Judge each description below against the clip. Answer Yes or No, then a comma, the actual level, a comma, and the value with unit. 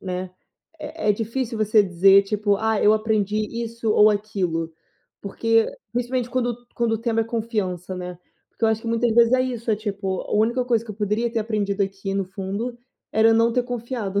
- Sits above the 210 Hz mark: Yes, high, 220 Hz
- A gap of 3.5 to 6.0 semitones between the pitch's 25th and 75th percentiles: No, average, 2.8 semitones